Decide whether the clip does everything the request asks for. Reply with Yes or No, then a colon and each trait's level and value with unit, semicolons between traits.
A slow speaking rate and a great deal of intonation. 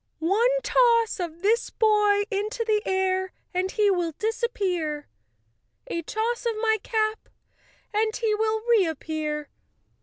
No: slow, 130 wpm; average, 3.5 semitones